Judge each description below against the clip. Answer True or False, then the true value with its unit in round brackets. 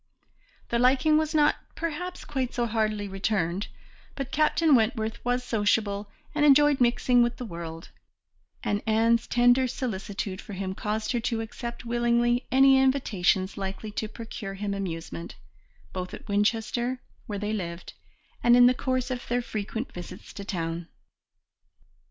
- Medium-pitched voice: False (230 Hz)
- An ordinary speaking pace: True (145 wpm)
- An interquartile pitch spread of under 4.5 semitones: True (3.9 semitones)